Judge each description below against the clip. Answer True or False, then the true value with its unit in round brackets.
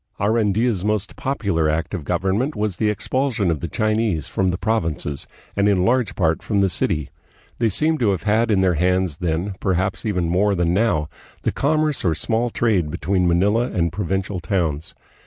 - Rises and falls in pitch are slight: False (4.1 semitones)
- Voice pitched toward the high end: False (95 Hz)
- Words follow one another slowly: False (180 wpm)